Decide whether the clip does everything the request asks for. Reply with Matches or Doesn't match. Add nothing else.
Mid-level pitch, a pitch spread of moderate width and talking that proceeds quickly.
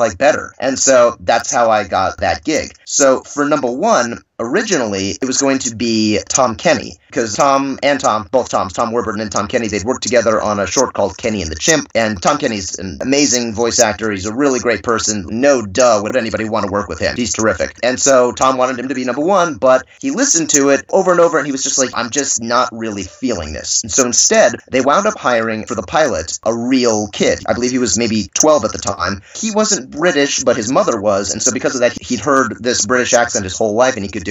Doesn't match